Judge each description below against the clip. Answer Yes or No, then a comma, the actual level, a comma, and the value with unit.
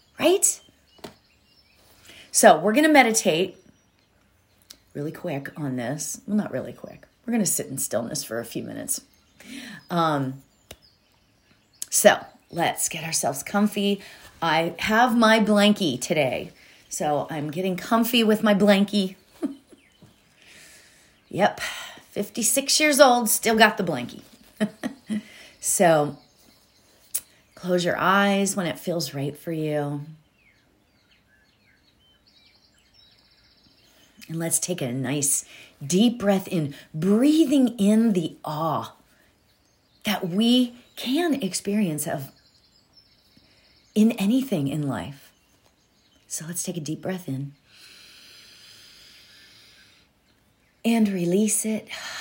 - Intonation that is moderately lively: No, wide, 7.2 semitones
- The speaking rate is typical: No, slow, 105 wpm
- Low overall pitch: No, medium, 185 Hz